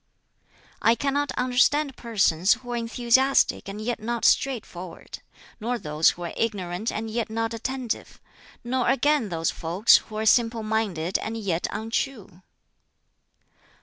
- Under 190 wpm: Yes, slow, 135 wpm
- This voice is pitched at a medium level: No, high, 225 Hz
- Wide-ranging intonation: No, average, 3.7 semitones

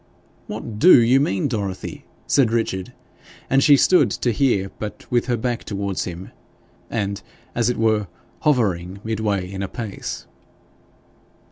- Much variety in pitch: No, average, 3.8 semitones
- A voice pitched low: Yes, low, 110 Hz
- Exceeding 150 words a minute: No, average, 140 wpm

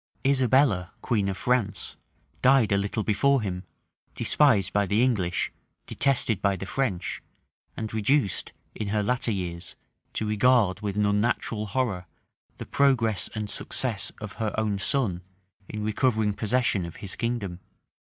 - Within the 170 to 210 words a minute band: No, average, 145 wpm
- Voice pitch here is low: Yes, low, 105 Hz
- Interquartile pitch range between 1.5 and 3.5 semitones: No, average, 3.9 semitones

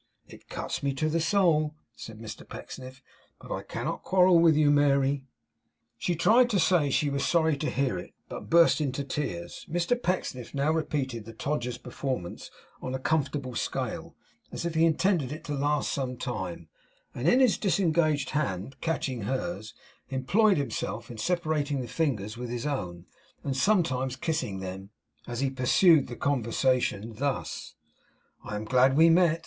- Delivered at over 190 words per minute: No, average, 165 wpm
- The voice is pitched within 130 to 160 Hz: Yes, medium, 140 Hz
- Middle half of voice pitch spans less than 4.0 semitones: No, average, 4.4 semitones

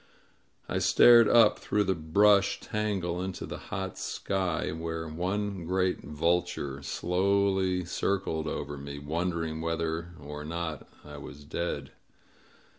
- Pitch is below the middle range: Yes, very low, 85 Hz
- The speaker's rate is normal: No, slow, 120 wpm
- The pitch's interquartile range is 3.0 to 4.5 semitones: Yes, average, 3.4 semitones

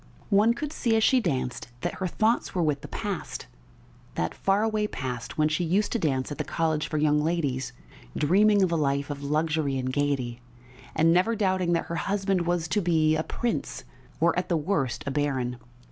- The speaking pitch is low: No, medium, 160 Hz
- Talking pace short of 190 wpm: No, average, 195 wpm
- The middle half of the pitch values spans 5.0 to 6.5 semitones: Yes, wide, 5.4 semitones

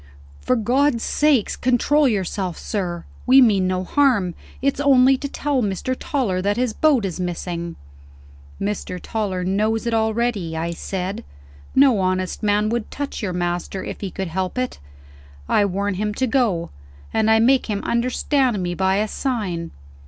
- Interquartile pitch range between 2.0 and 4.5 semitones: No, average, 5.3 semitones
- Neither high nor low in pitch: No, high, 210 Hz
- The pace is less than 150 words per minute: No, average, 160 wpm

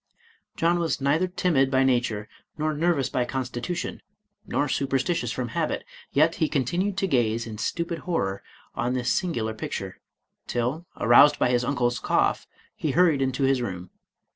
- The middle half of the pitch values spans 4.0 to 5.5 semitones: Yes, average, 5.2 semitones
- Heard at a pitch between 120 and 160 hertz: Yes, low, 135 Hz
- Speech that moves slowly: No, average, 155 wpm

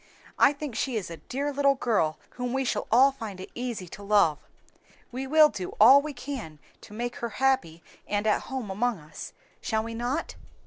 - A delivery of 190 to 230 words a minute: Yes, average, 195 wpm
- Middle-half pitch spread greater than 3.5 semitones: Yes, average, 4.6 semitones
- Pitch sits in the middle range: No, high, 240 Hz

